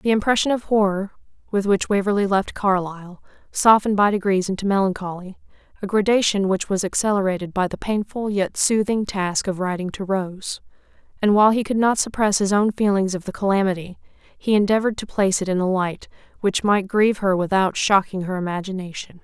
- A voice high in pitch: Yes, high, 195 Hz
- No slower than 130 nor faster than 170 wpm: No, average, 180 wpm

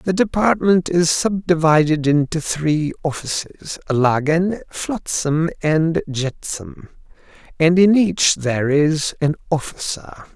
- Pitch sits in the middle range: Yes, medium, 160 Hz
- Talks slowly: Yes, slow, 95 wpm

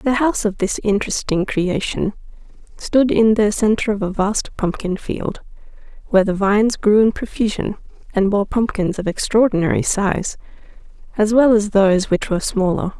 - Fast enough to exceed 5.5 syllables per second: No, 5.1 syllables/s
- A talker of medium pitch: No, high, 210 Hz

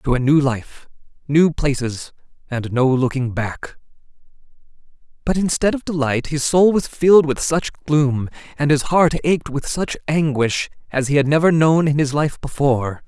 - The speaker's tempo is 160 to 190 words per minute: Yes, average, 170 wpm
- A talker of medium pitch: Yes, medium, 145 Hz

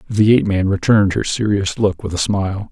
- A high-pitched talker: No, low, 100 Hz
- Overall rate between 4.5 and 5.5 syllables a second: No, 5.9 syllables/s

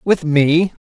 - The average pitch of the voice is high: No, medium, 160 Hz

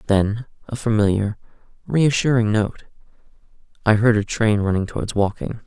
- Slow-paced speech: Yes, slow, 105 wpm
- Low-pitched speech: Yes, low, 110 Hz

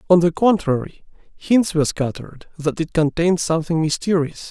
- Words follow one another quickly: No, average, 145 wpm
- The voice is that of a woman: No, male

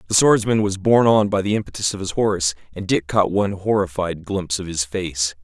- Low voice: Yes, very low, 95 Hz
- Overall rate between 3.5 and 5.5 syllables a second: No, 5.8 syllables/s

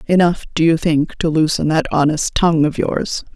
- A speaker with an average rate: Yes, average, 195 wpm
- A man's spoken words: No, female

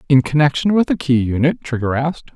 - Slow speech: No, fast, 205 wpm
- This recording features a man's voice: Yes, male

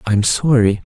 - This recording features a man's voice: Yes, male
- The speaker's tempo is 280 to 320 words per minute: No, average, 200 wpm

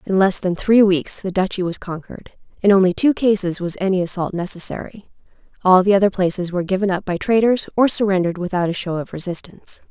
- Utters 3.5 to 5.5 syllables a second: No, 6.2 syllables/s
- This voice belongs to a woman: Yes, female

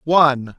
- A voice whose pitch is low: No, medium, 145 Hz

